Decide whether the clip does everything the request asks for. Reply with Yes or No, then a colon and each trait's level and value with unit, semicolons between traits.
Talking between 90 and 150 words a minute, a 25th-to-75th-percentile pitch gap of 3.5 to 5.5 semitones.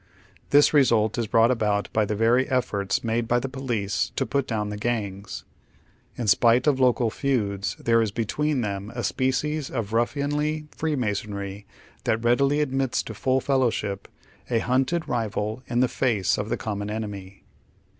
No: average, 165 wpm; average, 4.0 semitones